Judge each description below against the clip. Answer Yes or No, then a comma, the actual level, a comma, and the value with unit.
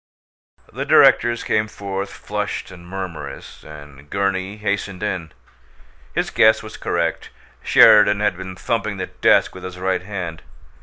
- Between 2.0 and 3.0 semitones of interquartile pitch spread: Yes, narrow, 2.5 semitones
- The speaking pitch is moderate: No, very low, 95 Hz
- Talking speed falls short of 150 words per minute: Yes, average, 140 wpm